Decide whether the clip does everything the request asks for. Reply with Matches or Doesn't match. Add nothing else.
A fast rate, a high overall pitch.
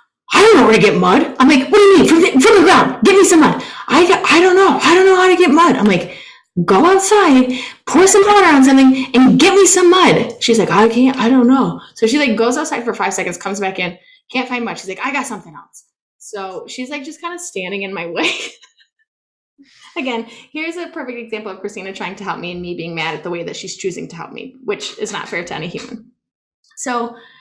Matches